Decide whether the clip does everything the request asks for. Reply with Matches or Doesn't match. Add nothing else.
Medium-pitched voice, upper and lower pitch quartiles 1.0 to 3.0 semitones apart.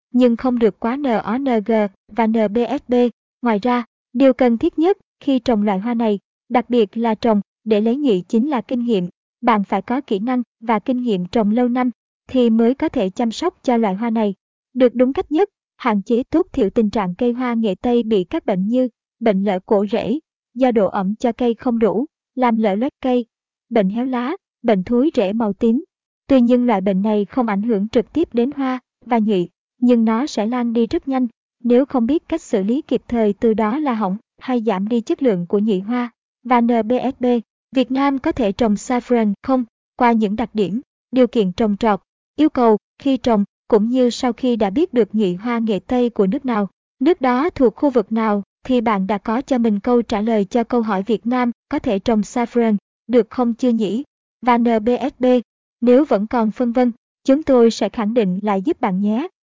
Doesn't match